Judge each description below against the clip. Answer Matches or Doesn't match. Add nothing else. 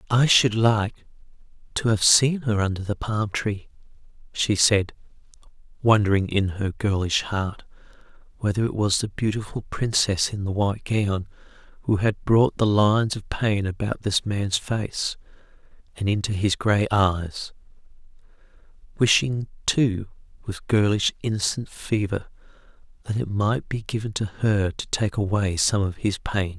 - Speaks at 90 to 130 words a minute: Doesn't match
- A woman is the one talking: Doesn't match